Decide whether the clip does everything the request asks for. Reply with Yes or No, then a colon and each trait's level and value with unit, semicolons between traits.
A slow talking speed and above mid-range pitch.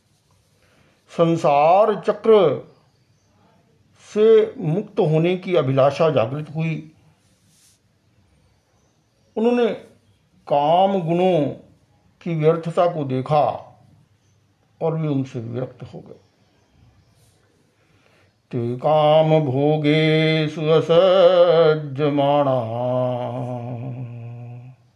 No: slow, 65 wpm; medium, 145 Hz